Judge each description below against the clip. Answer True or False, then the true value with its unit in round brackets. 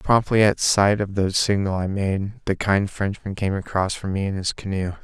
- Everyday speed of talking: False (215 wpm)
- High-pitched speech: False (100 Hz)